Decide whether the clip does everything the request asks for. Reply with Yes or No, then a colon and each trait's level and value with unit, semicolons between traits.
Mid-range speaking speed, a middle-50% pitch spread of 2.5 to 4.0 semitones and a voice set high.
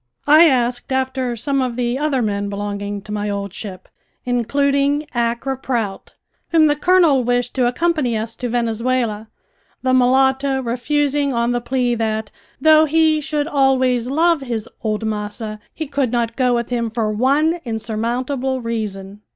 Yes: average, 155 wpm; average, 3.6 semitones; high, 245 Hz